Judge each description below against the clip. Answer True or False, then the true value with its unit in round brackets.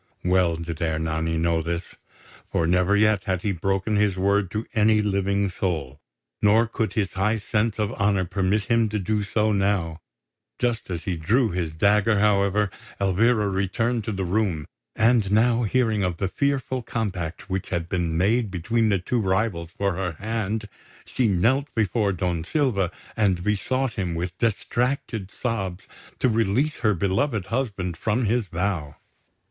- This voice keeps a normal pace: True (160 wpm)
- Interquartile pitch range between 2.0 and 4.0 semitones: True (3.6 semitones)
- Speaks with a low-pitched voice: True (100 Hz)